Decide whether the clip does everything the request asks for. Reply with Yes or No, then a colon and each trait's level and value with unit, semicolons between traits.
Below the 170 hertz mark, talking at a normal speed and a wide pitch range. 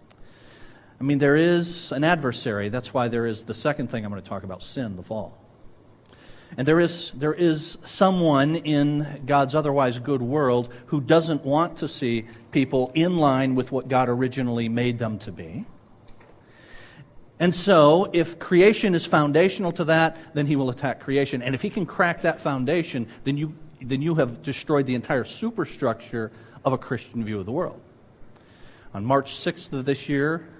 No: medium, 140 Hz; average, 175 wpm; average, 4.8 semitones